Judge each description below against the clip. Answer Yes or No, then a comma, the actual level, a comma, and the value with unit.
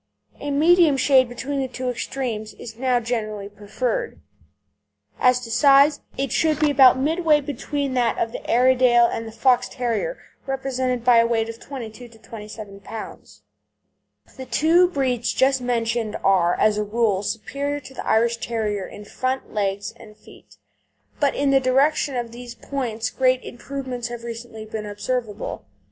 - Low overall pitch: No, high, 245 Hz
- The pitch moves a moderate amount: Yes, average, 3.3 semitones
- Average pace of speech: Yes, average, 160 wpm